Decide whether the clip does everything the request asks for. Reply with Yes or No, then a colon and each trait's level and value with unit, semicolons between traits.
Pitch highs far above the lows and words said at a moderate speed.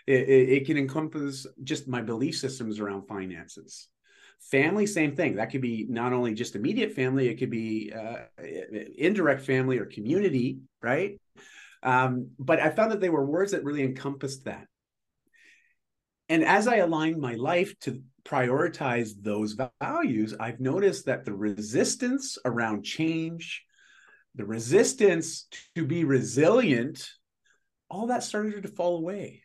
Yes: wide, 6.2 semitones; average, 145 wpm